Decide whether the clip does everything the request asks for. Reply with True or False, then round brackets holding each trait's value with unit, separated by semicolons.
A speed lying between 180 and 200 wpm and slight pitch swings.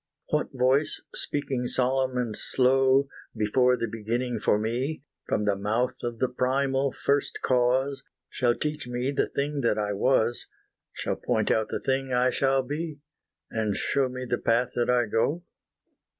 False (160 wpm; 2.2 semitones)